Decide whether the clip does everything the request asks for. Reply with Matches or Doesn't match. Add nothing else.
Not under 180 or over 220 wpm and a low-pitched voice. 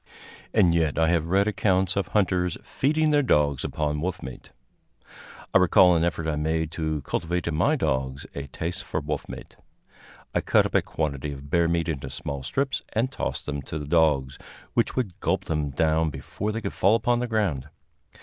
Matches